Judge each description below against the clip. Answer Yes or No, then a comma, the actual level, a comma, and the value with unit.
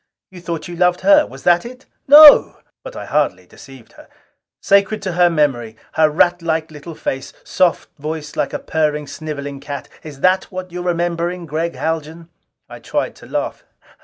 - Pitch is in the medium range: Yes, medium, 165 Hz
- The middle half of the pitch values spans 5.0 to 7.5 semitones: No, average, 3.1 semitones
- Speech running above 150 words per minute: Yes, average, 170 wpm